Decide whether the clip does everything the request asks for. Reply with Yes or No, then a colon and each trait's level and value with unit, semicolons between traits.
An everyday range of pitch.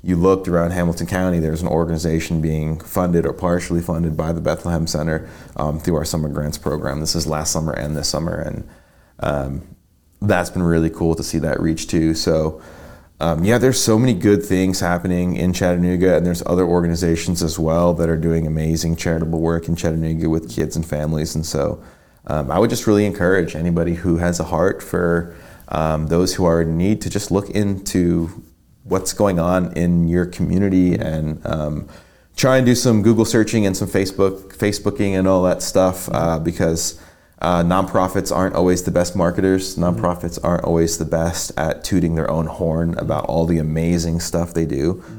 No: narrow, 2.2 semitones